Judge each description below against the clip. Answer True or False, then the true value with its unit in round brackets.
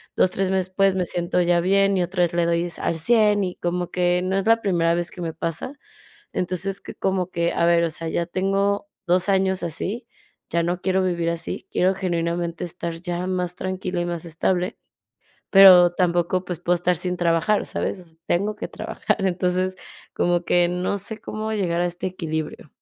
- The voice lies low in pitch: False (180 Hz)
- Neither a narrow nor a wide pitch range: False (1.7 semitones)